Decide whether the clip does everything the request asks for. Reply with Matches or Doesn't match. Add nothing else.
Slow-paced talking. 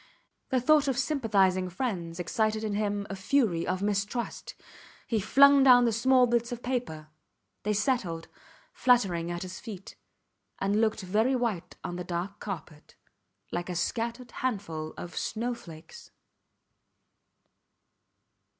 Matches